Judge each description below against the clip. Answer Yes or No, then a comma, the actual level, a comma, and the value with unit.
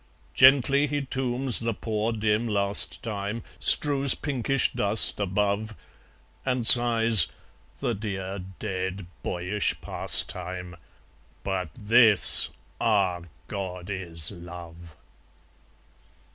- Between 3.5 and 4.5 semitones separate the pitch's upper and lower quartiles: Yes, average, 4.1 semitones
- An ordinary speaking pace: No, slow, 90 wpm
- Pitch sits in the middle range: No, low, 105 Hz